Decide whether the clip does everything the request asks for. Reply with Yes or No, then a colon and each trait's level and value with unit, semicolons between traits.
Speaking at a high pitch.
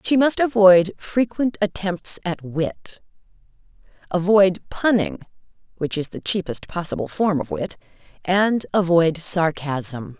No: medium, 180 Hz